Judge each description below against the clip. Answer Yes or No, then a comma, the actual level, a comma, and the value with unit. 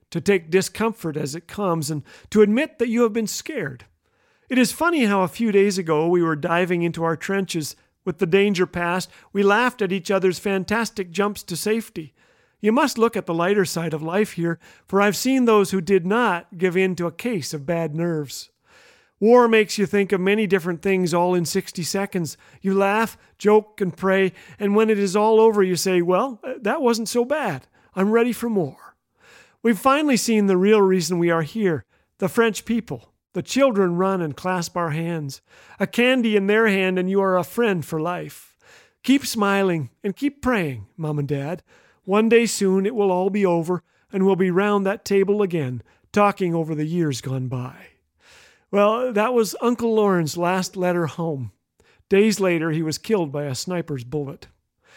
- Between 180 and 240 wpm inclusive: Yes, average, 195 wpm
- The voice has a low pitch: No, high, 195 Hz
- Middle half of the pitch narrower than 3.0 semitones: No, average, 3.9 semitones